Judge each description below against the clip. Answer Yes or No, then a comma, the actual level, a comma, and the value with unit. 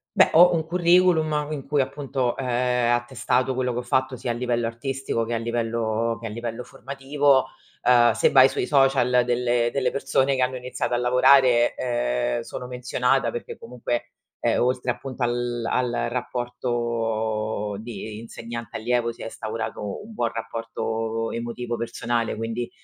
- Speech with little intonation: Yes, narrow, 2.0 semitones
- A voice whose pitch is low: Yes, low, 120 Hz